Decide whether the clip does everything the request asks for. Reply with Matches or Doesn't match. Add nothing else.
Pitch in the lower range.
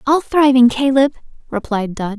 Doesn't match